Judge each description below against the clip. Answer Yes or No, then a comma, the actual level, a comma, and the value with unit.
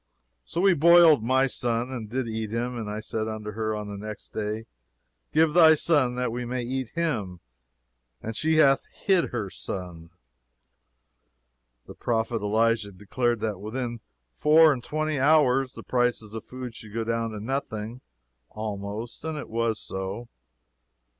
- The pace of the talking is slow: No, average, 160 wpm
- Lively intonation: No, average, 3.7 semitones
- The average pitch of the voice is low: Yes, low, 115 Hz